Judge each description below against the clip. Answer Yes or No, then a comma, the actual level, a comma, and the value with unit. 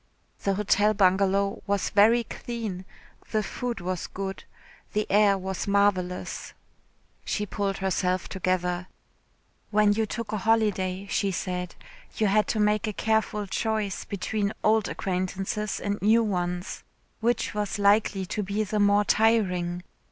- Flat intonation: Yes, narrow, 2.1 semitones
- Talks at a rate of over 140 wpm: No, slow, 135 wpm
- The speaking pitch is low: No, high, 200 Hz